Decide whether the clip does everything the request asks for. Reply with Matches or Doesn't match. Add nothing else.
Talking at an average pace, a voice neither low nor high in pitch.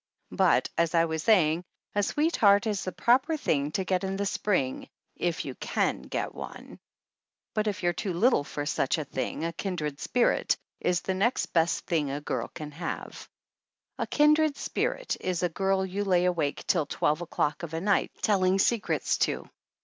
Matches